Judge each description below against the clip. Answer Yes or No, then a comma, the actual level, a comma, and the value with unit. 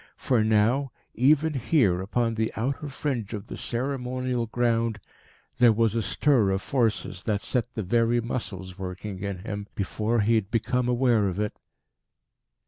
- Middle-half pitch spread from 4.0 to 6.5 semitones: No, average, 3.2 semitones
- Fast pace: No, average, 155 wpm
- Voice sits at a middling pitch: No, low, 115 Hz